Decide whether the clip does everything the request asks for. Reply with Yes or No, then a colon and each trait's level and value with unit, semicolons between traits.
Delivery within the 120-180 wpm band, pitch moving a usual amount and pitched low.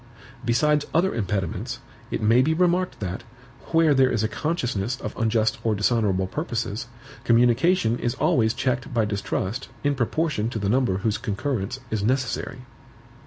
Yes: average, 150 wpm; average, 4.5 semitones; low, 120 Hz